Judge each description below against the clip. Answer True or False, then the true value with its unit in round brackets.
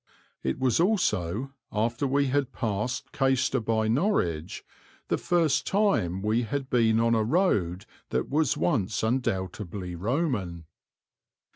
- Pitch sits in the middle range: False (115 Hz)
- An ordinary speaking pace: False (125 wpm)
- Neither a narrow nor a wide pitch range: False (6.0 semitones)